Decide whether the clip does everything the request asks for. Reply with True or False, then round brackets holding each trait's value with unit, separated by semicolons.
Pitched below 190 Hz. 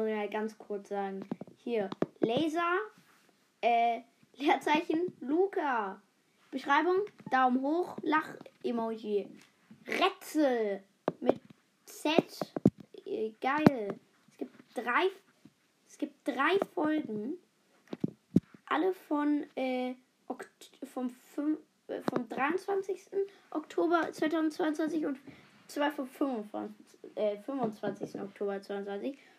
False (290 Hz)